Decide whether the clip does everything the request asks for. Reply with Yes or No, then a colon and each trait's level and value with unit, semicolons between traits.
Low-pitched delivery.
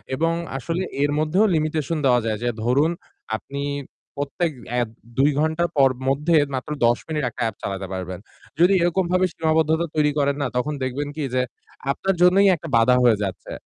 No: medium, 150 Hz